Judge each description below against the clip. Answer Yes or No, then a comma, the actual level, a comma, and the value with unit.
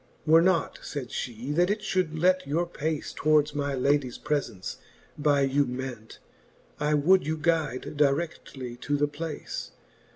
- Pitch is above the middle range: No, medium, 145 Hz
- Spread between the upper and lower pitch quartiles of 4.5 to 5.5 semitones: No, average, 2.8 semitones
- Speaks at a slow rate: No, average, 150 wpm